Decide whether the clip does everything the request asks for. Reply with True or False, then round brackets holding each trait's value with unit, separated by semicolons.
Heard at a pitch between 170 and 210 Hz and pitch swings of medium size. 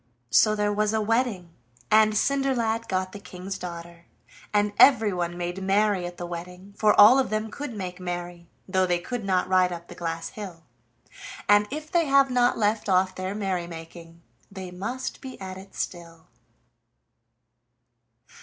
True (190 Hz; 3.5 semitones)